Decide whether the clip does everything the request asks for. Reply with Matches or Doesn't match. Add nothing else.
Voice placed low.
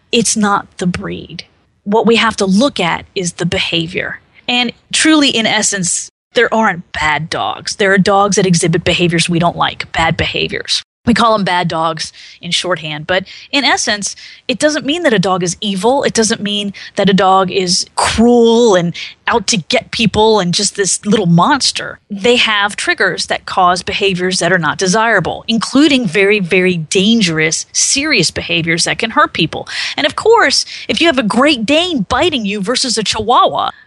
Doesn't match